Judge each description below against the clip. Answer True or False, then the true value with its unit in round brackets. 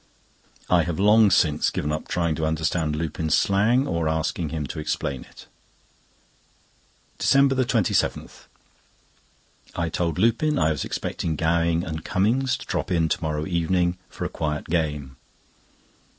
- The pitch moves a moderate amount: True (3.3 semitones)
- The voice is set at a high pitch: False (85 Hz)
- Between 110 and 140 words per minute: True (135 wpm)